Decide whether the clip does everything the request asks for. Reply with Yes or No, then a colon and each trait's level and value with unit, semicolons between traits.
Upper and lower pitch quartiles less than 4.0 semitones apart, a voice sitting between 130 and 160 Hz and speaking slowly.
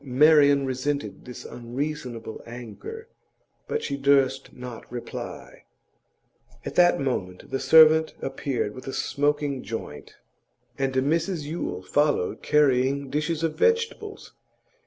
Yes: average, 3.5 semitones; medium, 140 Hz; slow, 115 wpm